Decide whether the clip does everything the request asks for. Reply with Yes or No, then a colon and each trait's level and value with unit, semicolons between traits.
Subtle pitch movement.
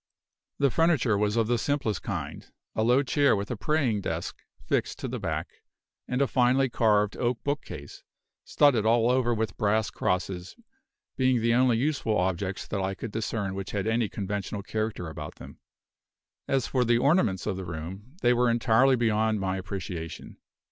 No: average, 4.1 semitones